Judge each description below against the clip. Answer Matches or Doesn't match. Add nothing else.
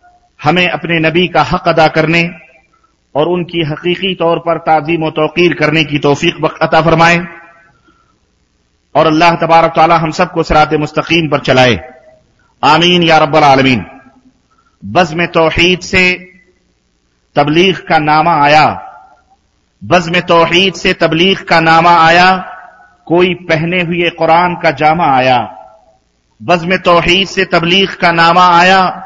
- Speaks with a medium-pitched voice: Matches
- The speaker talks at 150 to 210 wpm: Doesn't match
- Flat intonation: Matches